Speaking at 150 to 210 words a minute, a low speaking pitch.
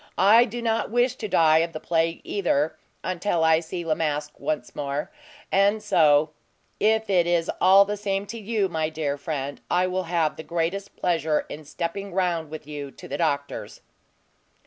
No: average, 180 wpm; medium, 170 Hz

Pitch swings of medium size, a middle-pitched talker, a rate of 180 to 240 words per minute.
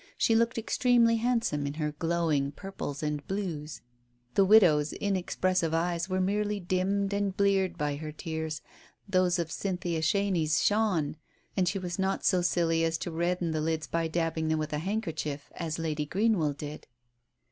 No: average, 3.8 semitones; medium, 170 Hz; average, 170 wpm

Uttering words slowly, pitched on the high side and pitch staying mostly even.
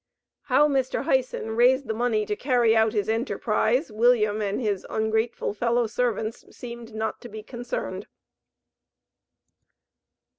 Yes: slow, 125 wpm; high, 230 Hz; narrow, 2.2 semitones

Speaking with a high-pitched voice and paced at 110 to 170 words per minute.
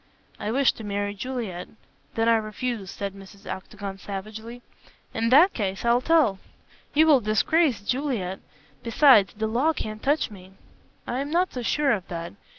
Yes: high, 220 Hz; average, 160 wpm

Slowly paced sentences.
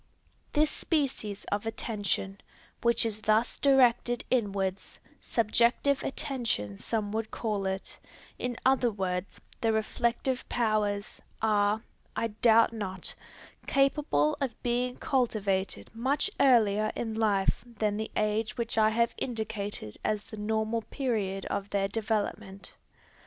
Yes: slow, 120 wpm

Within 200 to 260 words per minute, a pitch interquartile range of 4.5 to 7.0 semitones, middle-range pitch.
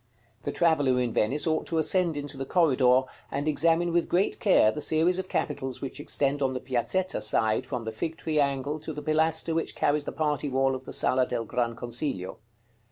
No: fast, 205 wpm; average, 3.9 semitones; medium, 145 Hz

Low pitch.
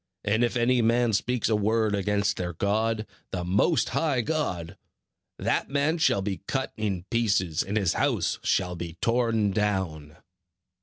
Yes: low, 105 Hz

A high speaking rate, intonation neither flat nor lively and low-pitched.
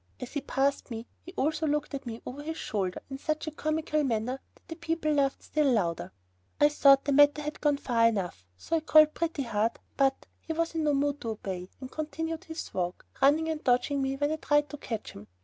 No: fast, 225 wpm; average, 4.1 semitones; very high, 285 Hz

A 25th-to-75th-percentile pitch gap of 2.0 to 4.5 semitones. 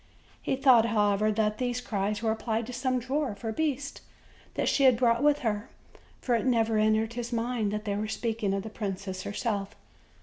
Yes: average, 2.8 semitones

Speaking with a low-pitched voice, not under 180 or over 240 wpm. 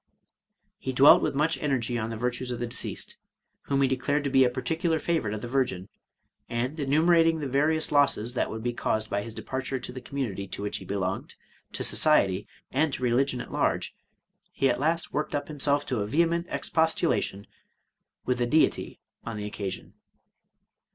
Yes: low, 130 Hz; average, 190 wpm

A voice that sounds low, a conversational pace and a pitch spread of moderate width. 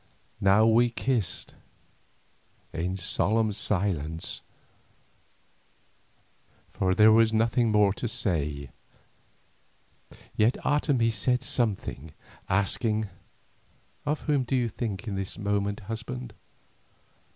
No: low, 105 Hz; slow, 95 wpm; average, 3.3 semitones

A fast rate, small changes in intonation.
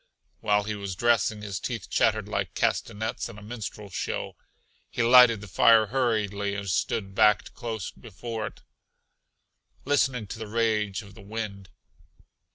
No: average, 150 wpm; narrow, 2.2 semitones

